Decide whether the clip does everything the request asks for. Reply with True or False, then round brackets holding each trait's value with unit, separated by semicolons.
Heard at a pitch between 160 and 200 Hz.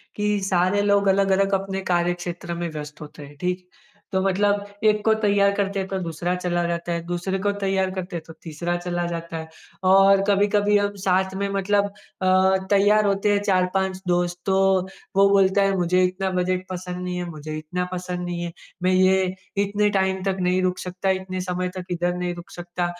True (185 Hz)